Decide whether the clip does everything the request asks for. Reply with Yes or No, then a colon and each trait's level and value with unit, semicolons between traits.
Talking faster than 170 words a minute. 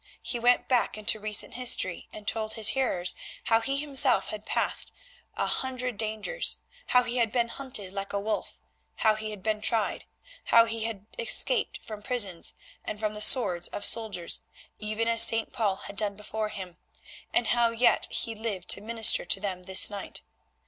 Yes: average, 180 wpm